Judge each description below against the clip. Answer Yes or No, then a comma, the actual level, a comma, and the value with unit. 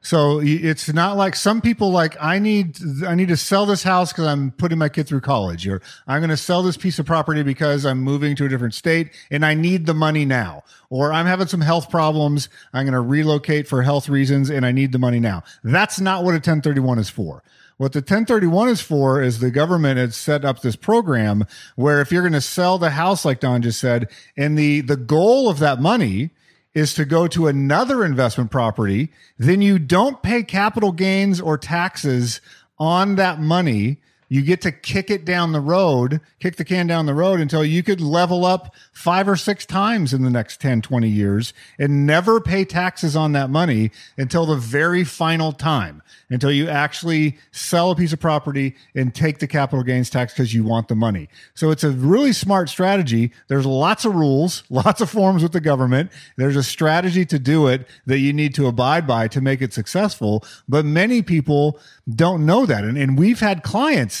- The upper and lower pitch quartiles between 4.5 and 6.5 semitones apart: Yes, average, 4.9 semitones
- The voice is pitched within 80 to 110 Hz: No, medium, 150 Hz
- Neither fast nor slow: No, fast, 210 wpm